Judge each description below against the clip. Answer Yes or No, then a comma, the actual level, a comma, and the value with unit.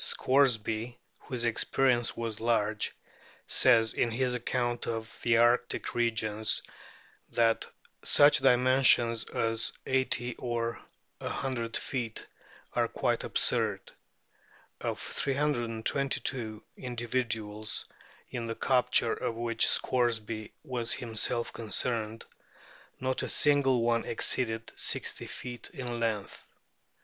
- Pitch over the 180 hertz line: No, low, 120 Hz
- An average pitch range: No, narrow, 1.9 semitones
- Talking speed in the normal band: No, slow, 105 wpm